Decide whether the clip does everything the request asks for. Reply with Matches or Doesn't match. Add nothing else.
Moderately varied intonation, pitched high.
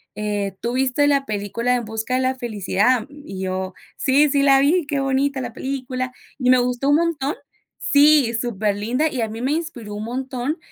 Matches